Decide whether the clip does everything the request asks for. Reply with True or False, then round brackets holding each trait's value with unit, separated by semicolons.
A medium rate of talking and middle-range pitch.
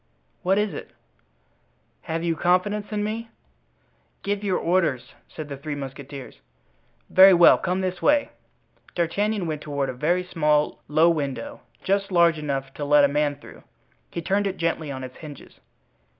True (160 wpm; 165 Hz)